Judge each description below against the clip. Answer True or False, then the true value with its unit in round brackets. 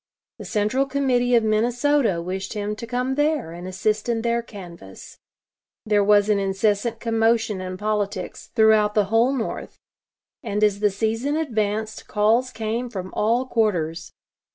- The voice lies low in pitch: False (215 Hz)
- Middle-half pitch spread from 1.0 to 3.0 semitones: True (2.6 semitones)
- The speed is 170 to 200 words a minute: False (150 wpm)